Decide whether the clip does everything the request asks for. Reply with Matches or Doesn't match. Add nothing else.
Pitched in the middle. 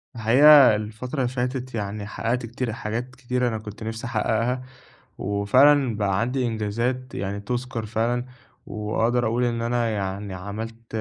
Doesn't match